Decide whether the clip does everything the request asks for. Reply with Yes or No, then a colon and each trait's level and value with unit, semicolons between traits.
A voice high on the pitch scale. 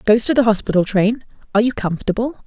Yes: high, 220 Hz